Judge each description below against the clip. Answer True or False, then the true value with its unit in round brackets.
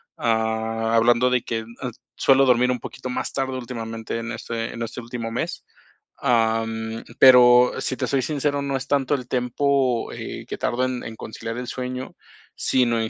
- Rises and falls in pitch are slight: True (2.1 semitones)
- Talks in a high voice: False (120 Hz)